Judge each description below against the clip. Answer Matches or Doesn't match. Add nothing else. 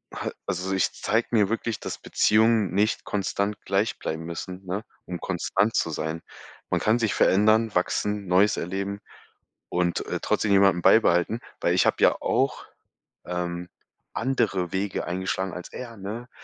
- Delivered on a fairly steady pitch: Doesn't match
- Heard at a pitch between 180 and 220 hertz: Doesn't match